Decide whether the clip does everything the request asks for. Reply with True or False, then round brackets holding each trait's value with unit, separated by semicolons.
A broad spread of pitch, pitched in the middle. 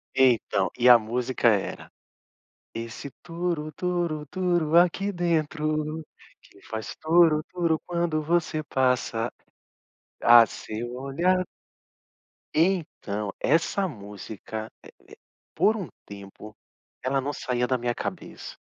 True (6.2 semitones; 150 Hz)